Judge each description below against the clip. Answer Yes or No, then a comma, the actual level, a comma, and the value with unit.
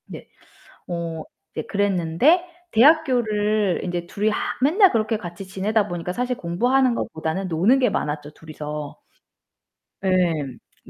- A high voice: Yes, high, 195 Hz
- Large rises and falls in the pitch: Yes, wide, 5.8 semitones